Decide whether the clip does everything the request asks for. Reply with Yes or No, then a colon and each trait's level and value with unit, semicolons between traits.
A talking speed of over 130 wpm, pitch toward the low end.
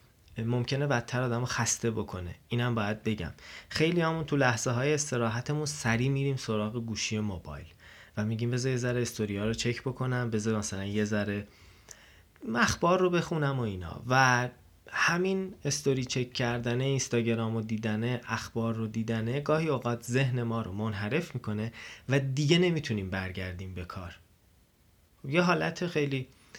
Yes: average, 145 wpm; low, 120 Hz